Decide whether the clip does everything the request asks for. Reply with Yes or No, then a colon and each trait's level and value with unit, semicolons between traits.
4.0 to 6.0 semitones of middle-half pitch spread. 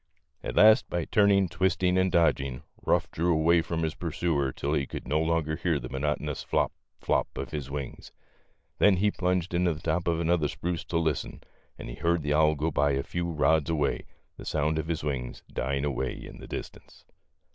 No: average, 2.9 semitones